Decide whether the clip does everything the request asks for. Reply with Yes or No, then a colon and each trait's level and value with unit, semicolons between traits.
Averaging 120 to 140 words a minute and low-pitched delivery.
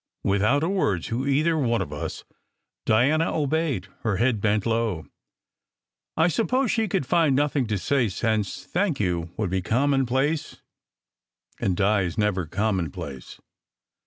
Yes: slow, 135 wpm; low, 115 Hz